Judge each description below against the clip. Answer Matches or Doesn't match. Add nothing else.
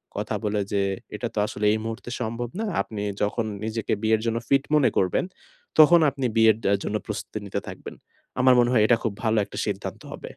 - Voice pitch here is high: Doesn't match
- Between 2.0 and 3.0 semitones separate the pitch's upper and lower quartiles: Matches